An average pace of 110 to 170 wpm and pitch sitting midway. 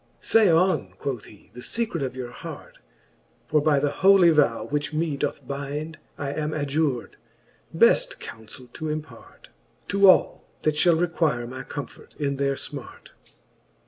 Yes: average, 150 wpm; medium, 150 Hz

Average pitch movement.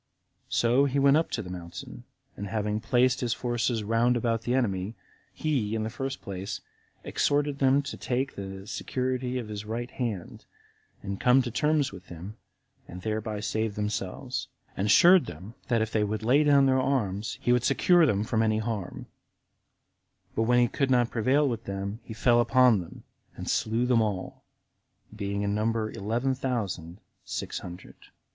Yes: average, 3.8 semitones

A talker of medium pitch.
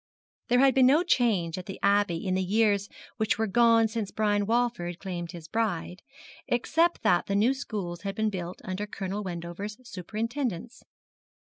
No: high, 205 Hz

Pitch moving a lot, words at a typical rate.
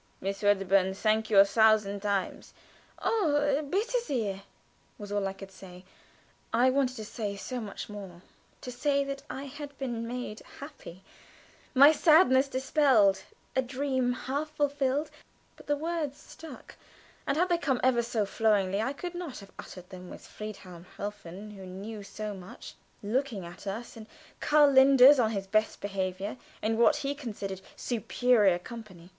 Yes: wide, 5.8 semitones; average, 160 wpm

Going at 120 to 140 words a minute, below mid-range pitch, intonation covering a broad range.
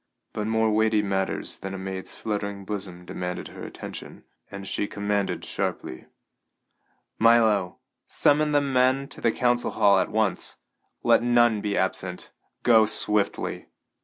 No: slow, 135 wpm; low, 105 Hz; average, 3.0 semitones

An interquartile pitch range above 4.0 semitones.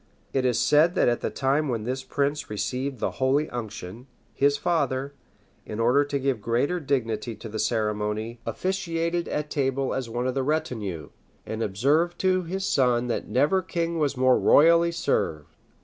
Yes: average, 4.7 semitones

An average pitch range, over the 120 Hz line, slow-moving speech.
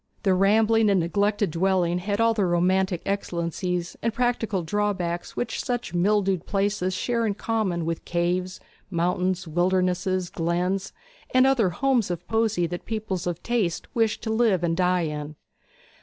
No: average, 3.6 semitones; medium, 185 Hz; average, 150 wpm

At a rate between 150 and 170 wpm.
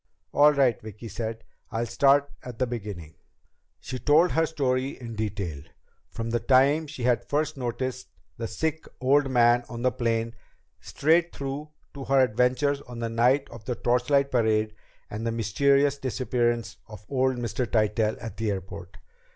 Yes: average, 160 wpm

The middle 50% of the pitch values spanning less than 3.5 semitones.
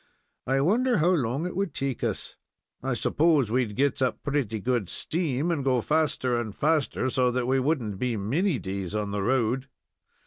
No: average, 4.8 semitones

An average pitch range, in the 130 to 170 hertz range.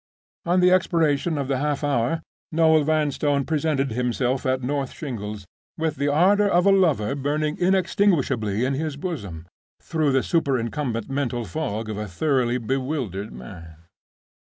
Yes: average, 4.7 semitones; medium, 140 Hz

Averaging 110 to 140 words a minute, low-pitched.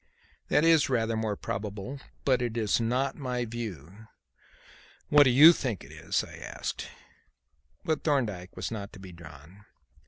No: average, 155 wpm; low, 115 Hz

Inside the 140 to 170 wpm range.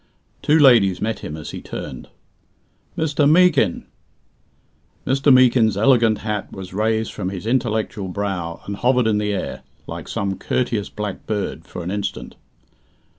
Yes: average, 145 wpm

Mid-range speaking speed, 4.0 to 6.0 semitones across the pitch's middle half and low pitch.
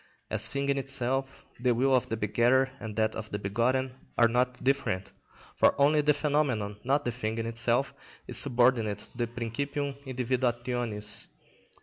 No: average, 160 wpm; average, 2.9 semitones; low, 125 Hz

